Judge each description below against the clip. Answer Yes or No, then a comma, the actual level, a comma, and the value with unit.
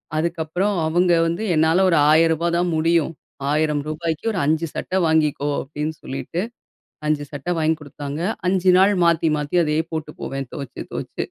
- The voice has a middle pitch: Yes, medium, 160 Hz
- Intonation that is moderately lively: No, narrow, 2.1 semitones